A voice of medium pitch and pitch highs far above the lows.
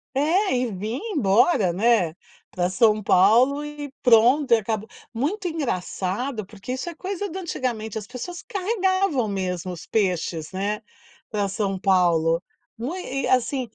No: high, 230 Hz; wide, 7.1 semitones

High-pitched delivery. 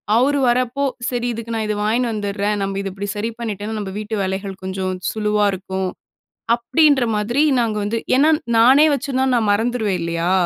Yes: high, 215 Hz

